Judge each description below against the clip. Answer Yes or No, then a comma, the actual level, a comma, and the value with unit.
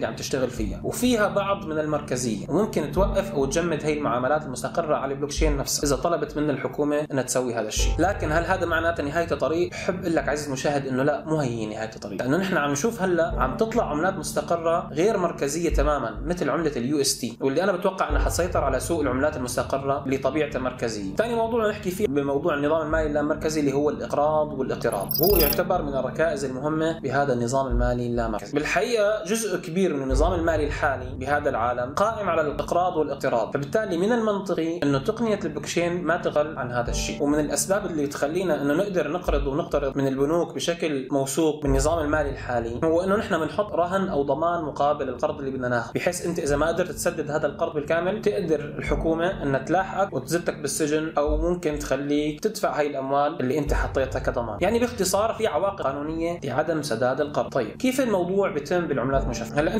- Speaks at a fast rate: Yes, fast, 180 wpm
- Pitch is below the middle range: No, medium, 150 Hz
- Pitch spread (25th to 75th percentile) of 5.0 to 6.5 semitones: No, average, 4.1 semitones